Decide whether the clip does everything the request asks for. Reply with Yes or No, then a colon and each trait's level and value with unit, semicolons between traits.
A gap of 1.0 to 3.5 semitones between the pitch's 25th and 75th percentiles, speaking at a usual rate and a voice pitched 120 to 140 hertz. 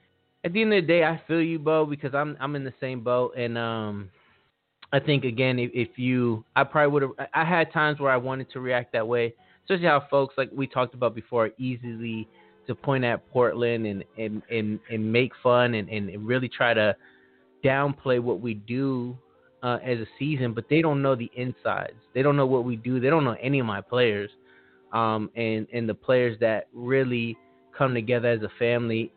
No: average, 3.1 semitones; fast, 210 wpm; low, 125 Hz